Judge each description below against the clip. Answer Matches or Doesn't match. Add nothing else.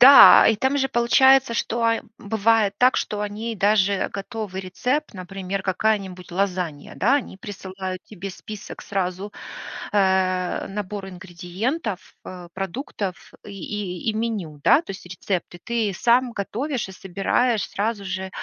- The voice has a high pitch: Matches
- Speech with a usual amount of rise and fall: Matches